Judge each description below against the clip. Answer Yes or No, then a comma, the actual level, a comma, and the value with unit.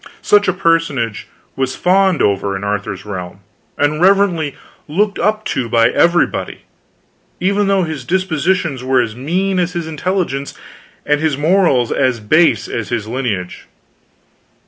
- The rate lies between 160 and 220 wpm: No, average, 140 wpm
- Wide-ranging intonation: Yes, wide, 7.5 semitones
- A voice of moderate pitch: Yes, medium, 150 Hz